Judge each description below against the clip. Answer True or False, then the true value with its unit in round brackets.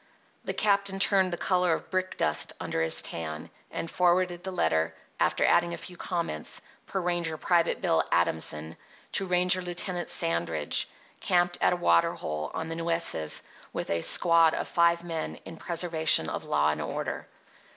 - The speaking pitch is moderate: True (170 Hz)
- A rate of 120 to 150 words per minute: False (165 wpm)